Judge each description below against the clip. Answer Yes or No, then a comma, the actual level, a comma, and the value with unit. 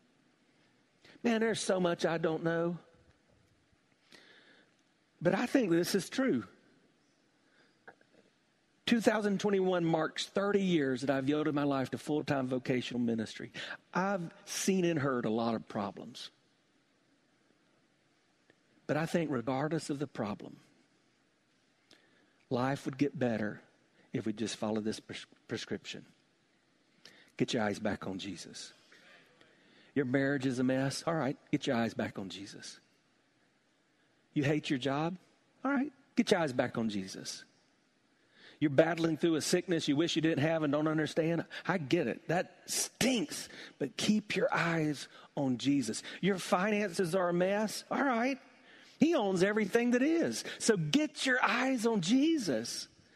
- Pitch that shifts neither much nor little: No, wide, 6.9 semitones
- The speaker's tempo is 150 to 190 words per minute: No, average, 140 wpm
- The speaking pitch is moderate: Yes, medium, 165 Hz